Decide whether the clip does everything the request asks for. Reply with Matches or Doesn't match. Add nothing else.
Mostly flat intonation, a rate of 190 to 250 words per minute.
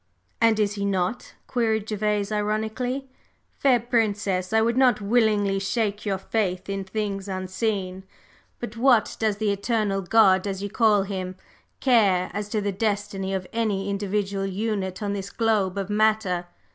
Doesn't match